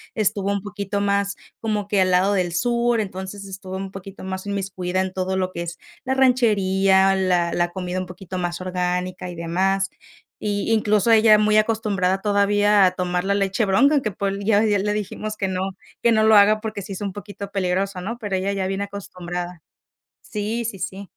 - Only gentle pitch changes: Yes, narrow, 2.1 semitones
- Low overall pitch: No, high, 195 Hz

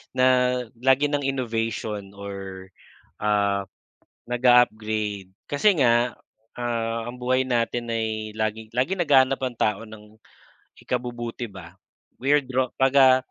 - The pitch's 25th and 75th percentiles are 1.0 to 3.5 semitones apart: Yes, average, 3.1 semitones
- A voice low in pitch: Yes, low, 120 Hz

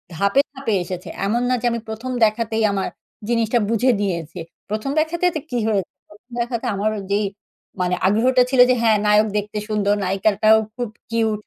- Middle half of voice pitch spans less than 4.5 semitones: Yes, average, 2.9 semitones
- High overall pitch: Yes, high, 215 Hz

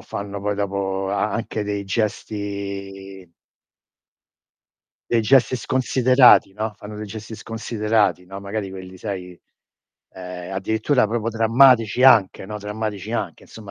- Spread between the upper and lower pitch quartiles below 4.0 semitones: Yes, narrow, 2.4 semitones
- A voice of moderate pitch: No, low, 105 Hz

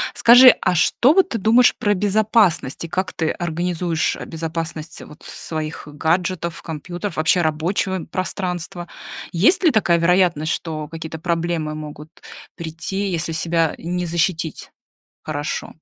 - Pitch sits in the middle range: Yes, medium, 170 Hz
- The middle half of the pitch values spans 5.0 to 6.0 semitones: No, average, 2.8 semitones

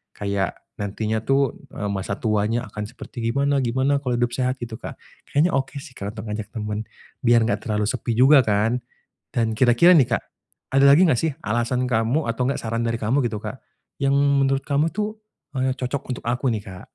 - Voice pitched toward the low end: Yes, low, 120 Hz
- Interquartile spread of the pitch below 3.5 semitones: No, average, 3.8 semitones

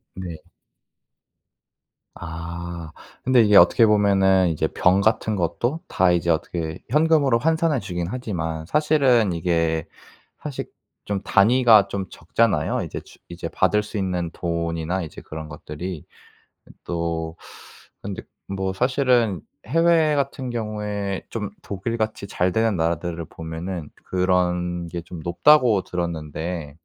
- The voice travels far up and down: No, average, 5.0 semitones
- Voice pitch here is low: Yes, very low, 95 Hz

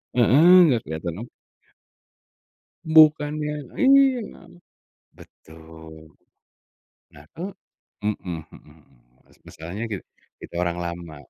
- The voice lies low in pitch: Yes, low, 100 Hz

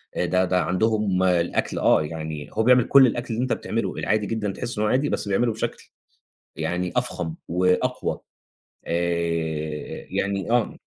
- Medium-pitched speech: No, very low, 95 Hz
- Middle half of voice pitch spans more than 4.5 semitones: Yes, average, 4.9 semitones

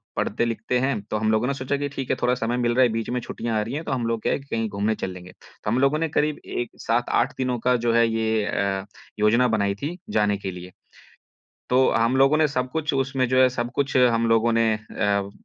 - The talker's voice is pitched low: Yes, low, 120 Hz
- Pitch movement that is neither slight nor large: Yes, average, 3.1 semitones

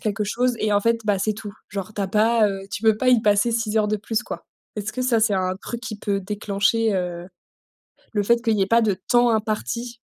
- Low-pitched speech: No, high, 215 Hz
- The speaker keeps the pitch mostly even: Yes, narrow, 2.3 semitones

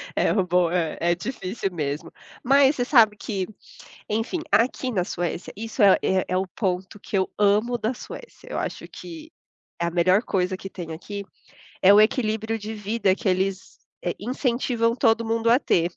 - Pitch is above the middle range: Yes, high, 205 Hz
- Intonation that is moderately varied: Yes, average, 3.9 semitones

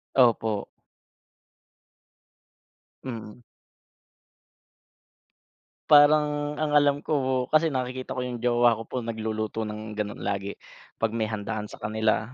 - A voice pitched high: No, low, 120 Hz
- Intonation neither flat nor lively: Yes, average, 3.5 semitones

